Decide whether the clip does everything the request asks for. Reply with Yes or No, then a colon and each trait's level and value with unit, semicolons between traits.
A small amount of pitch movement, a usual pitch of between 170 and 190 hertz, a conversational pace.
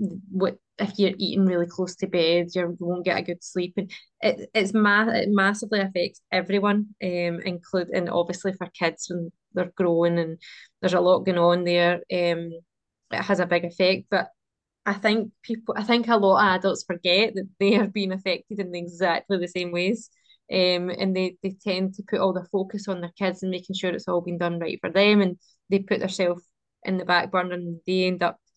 No: narrow, 2.1 semitones; medium, 185 Hz; fast, 210 wpm